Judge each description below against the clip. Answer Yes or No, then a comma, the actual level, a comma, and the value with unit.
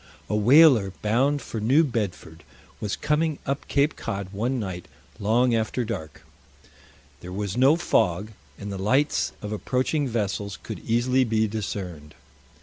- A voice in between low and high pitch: No, low, 110 Hz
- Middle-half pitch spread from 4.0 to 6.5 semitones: Yes, average, 4.7 semitones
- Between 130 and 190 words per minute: Yes, average, 145 wpm